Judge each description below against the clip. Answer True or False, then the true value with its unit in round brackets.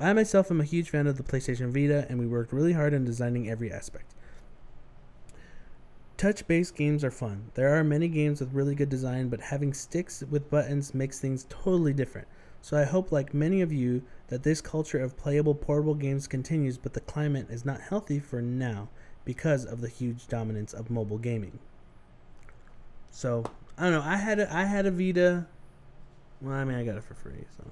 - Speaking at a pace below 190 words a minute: False (195 wpm)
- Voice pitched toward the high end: False (135 Hz)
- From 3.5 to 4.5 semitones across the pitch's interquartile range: True (4.0 semitones)